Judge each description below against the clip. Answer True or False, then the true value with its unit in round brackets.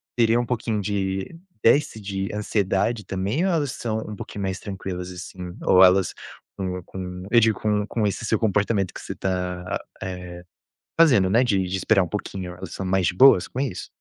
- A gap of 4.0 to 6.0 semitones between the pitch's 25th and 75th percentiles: False (3.2 semitones)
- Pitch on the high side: False (100 Hz)